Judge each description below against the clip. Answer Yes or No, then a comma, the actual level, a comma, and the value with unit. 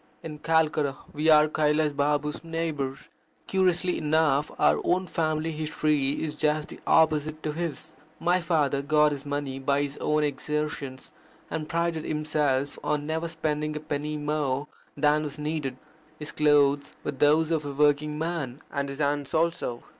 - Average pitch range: No, narrow, 1.6 semitones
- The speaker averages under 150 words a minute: No, average, 155 wpm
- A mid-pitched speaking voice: Yes, medium, 150 Hz